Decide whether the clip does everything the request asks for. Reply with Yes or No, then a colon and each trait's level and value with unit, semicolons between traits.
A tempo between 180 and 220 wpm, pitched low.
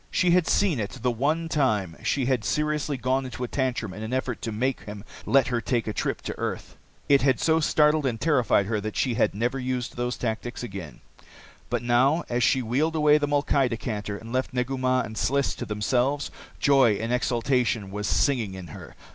Yes: fast, 205 wpm; low, 125 Hz